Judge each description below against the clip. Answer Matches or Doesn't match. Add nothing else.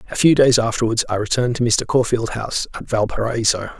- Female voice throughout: Doesn't match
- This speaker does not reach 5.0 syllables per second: Doesn't match